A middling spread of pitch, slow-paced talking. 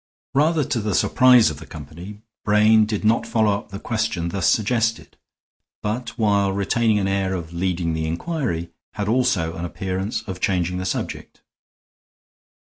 No: average, 3.9 semitones; average, 155 wpm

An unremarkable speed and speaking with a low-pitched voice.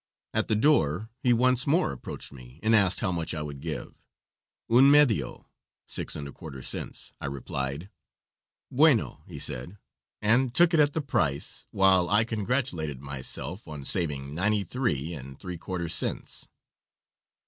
Yes: average, 155 wpm; very low, 90 Hz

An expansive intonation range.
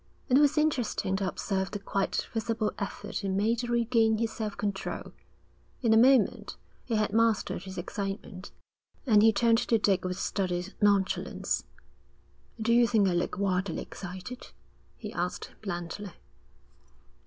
No: average, 3.0 semitones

